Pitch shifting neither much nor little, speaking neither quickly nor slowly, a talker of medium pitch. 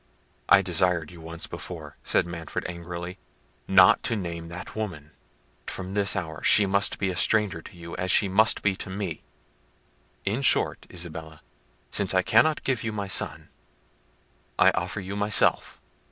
No: average, 3.1 semitones; average, 160 wpm; very low, 95 Hz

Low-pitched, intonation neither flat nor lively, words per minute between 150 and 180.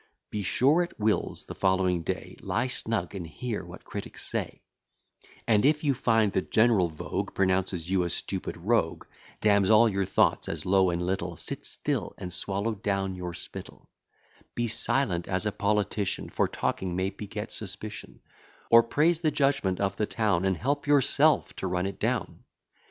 Yes: low, 100 Hz; average, 3.8 semitones; average, 170 wpm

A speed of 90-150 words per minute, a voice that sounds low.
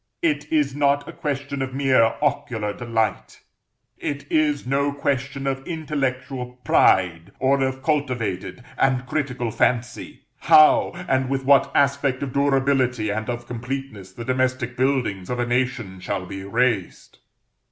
Yes: average, 140 wpm; low, 130 Hz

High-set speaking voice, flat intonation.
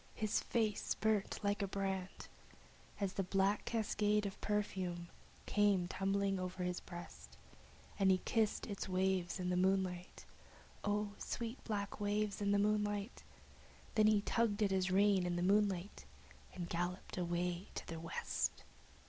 Yes: high, 195 Hz; narrow, 2.2 semitones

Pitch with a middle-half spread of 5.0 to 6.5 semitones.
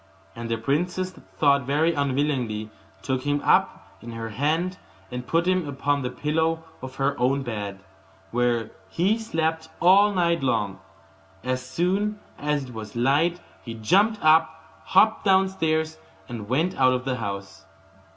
Yes: wide, 5.5 semitones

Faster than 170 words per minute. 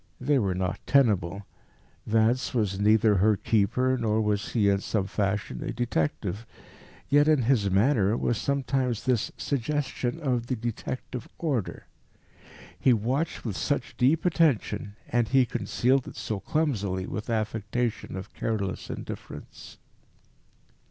No: slow, 135 wpm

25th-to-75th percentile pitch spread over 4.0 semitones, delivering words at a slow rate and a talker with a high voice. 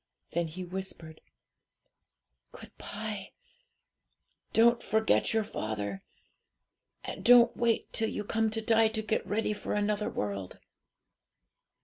Yes: average, 4.5 semitones; slow, 115 wpm; high, 210 Hz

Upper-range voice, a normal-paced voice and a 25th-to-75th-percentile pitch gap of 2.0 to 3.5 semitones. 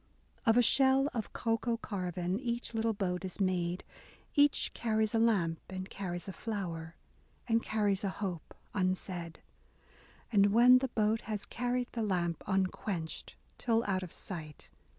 No: high, 200 Hz; average, 150 wpm; average, 4.0 semitones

